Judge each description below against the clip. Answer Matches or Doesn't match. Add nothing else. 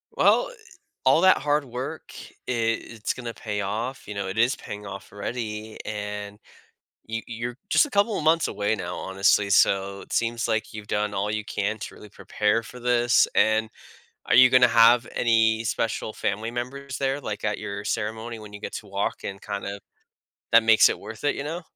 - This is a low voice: Matches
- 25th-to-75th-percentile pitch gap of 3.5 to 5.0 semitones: Doesn't match